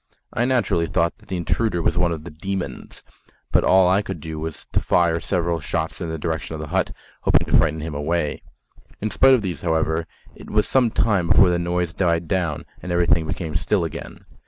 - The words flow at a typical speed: No, fast, 210 wpm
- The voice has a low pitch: Yes, very low, 85 Hz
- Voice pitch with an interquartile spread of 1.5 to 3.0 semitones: Yes, narrow, 2.6 semitones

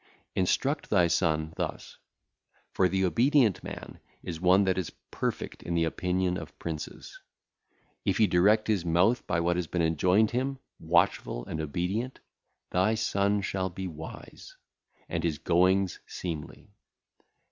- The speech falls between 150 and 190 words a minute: No, average, 140 wpm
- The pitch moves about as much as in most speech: Yes, average, 3.0 semitones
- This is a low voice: Yes, very low, 90 Hz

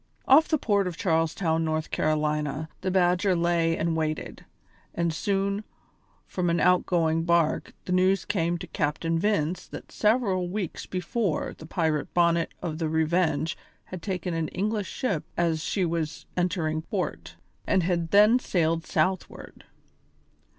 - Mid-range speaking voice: Yes, medium, 170 Hz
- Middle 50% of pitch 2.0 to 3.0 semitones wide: Yes, average, 2.7 semitones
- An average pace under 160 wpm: Yes, average, 145 wpm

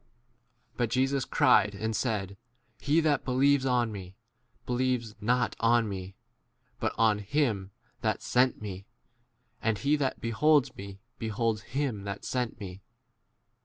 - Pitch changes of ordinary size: Yes, average, 4.0 semitones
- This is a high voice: No, low, 115 Hz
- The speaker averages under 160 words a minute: Yes, average, 145 wpm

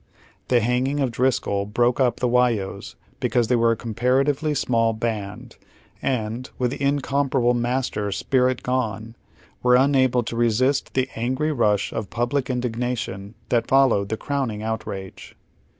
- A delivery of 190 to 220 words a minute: No, average, 150 wpm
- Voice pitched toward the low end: Yes, low, 125 Hz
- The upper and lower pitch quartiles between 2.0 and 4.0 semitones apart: Yes, narrow, 2.5 semitones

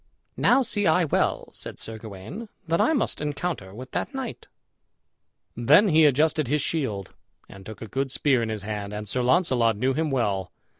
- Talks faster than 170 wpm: Yes, average, 185 wpm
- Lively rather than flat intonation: Yes, wide, 6.8 semitones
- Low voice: Yes, low, 130 Hz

